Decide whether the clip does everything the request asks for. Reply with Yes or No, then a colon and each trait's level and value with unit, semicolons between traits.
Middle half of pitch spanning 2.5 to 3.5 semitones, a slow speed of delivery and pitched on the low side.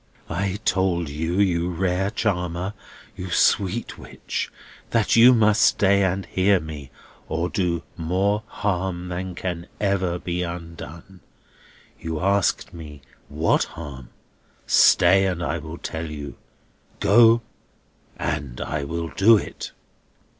Yes: average, 3.0 semitones; slow, 125 wpm; very low, 90 Hz